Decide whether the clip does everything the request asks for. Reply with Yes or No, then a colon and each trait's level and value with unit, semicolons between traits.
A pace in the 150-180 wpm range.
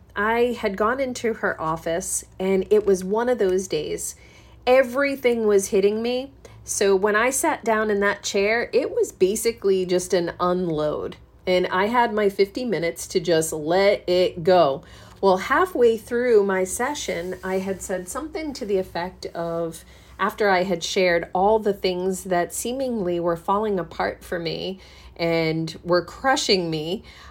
Yes: average, 160 wpm